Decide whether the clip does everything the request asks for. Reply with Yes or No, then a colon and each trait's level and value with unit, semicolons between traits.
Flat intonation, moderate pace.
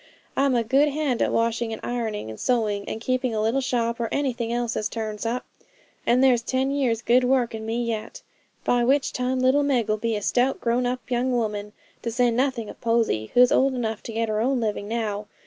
No: narrow, 2.3 semitones; fast, 215 wpm